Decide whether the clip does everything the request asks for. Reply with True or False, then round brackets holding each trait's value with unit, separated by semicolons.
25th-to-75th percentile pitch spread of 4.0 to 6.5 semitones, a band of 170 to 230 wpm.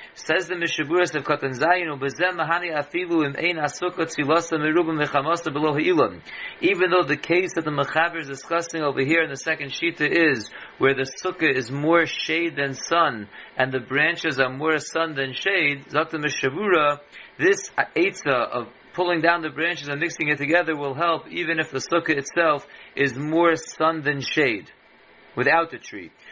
False (2.9 semitones; 180 wpm)